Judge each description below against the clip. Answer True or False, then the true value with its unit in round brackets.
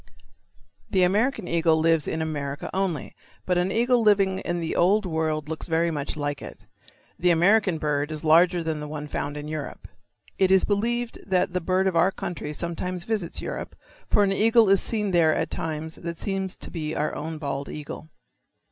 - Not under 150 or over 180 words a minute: False (190 wpm)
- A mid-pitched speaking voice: True (170 Hz)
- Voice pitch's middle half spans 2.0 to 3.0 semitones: False (3.7 semitones)